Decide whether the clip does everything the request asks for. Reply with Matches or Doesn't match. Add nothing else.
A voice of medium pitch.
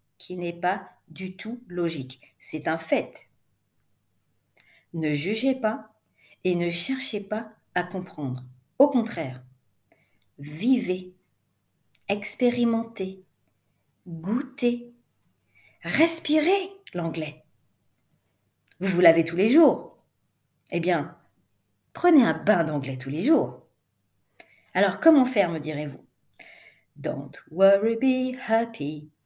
Matches